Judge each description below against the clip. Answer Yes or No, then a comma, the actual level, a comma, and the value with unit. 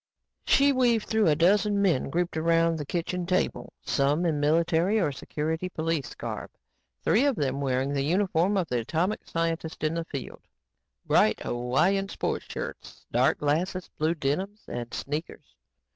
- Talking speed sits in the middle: Yes, average, 155 wpm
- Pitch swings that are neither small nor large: Yes, average, 4.2 semitones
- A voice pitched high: No, medium, 165 Hz